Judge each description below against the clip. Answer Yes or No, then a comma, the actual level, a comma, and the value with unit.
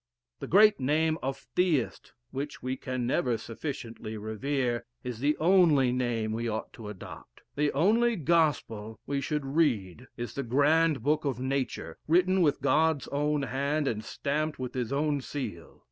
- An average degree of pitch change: Yes, average, 4.2 semitones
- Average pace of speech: Yes, average, 160 wpm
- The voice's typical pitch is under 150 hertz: Yes, medium, 140 Hz